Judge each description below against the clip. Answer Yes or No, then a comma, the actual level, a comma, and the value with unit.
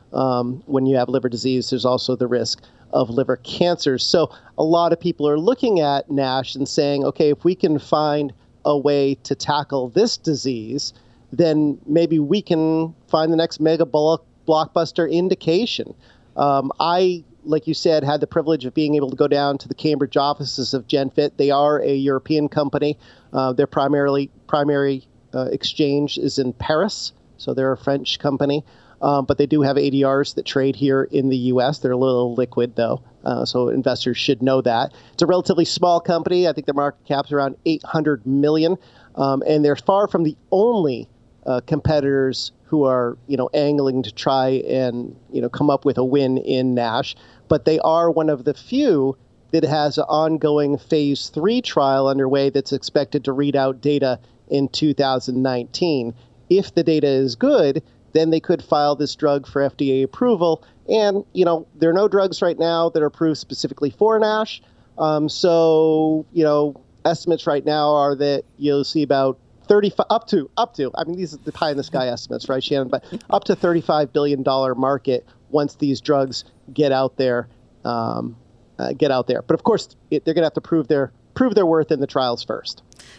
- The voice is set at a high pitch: No, medium, 145 Hz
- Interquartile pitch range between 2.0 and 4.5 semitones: Yes, average, 3.2 semitones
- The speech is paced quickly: No, average, 190 wpm